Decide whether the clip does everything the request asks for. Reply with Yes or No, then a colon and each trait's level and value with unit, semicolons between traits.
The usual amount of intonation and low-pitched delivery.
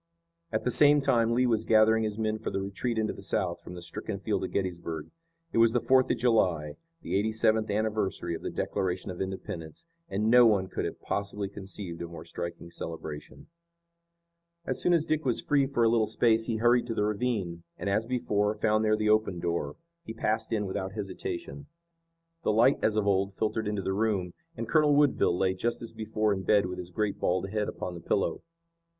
Yes: average, 3.2 semitones; low, 105 Hz